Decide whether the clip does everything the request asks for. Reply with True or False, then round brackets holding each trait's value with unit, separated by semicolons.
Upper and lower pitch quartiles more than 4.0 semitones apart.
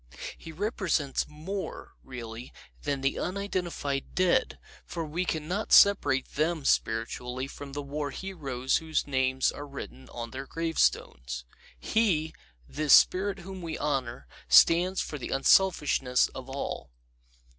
True (4.9 semitones)